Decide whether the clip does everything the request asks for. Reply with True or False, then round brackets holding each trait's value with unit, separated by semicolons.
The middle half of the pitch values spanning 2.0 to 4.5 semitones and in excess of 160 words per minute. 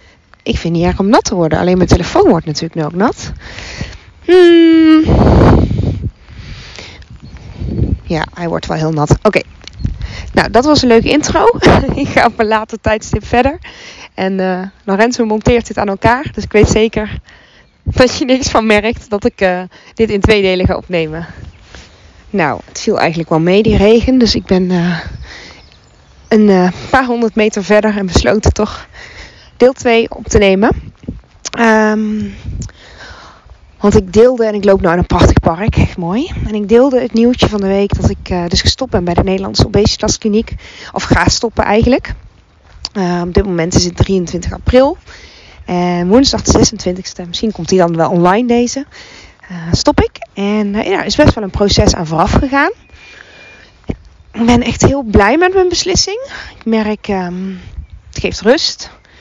False (4.9 semitones; 175 wpm)